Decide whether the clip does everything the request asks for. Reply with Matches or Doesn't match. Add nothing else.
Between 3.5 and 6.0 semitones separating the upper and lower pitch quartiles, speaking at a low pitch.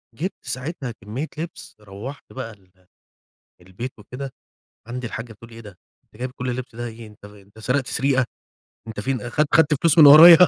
Matches